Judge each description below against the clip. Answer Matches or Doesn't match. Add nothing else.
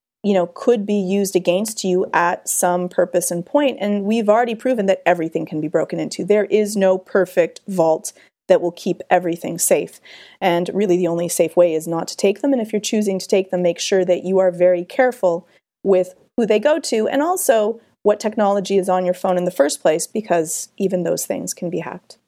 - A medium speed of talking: Doesn't match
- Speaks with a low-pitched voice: Doesn't match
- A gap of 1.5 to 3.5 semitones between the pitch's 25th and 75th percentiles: Matches